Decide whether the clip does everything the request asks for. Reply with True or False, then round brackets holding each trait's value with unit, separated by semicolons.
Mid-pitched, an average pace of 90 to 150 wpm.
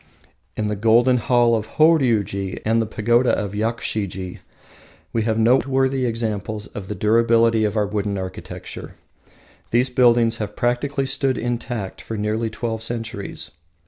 False (115 Hz; 140 wpm)